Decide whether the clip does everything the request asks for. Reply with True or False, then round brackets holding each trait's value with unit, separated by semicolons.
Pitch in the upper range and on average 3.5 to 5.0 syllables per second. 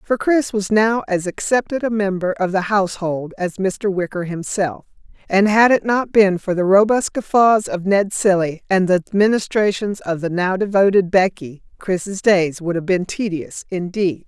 True (195 Hz; 4.5 syllables/s)